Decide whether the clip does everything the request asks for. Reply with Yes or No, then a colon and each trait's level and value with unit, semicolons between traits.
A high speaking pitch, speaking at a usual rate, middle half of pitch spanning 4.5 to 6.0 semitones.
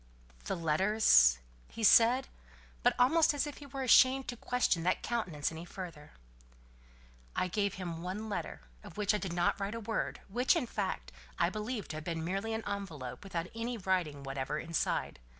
Yes: high, 195 Hz; average, 180 wpm; wide, 5.5 semitones